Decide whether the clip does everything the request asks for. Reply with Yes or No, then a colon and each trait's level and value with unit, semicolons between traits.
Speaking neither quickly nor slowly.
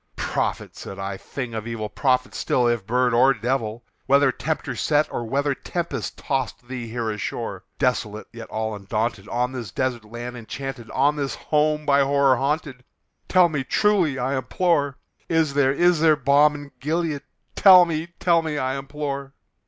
Yes: average, 170 wpm